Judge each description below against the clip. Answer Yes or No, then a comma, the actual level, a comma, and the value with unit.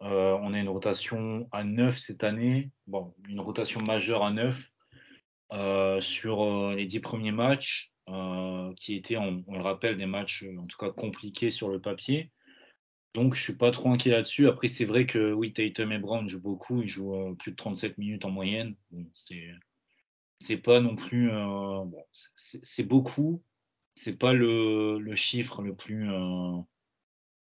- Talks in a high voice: No, low, 105 Hz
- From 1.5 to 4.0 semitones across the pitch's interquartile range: Yes, average, 3.5 semitones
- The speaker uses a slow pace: No, average, 180 wpm